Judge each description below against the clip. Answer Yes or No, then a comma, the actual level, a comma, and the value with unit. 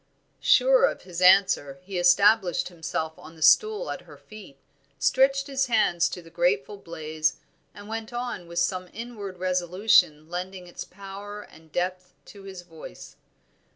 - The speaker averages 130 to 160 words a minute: Yes, average, 155 wpm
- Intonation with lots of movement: No, average, 3.7 semitones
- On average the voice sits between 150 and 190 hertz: Yes, medium, 185 Hz